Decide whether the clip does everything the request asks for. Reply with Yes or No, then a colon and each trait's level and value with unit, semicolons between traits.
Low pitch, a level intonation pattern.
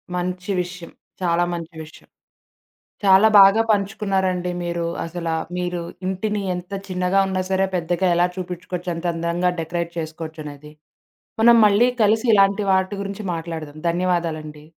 No: medium, 180 Hz; narrow, 2.3 semitones